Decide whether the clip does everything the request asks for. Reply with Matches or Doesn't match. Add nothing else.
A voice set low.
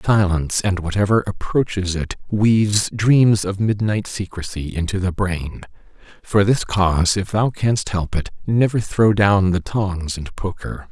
Matches